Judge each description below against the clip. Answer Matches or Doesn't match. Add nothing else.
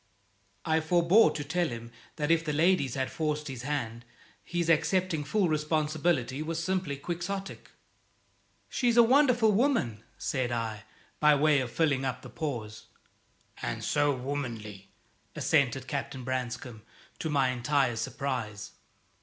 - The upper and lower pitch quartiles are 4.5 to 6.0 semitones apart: Matches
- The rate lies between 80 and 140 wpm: Matches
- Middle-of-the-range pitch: Matches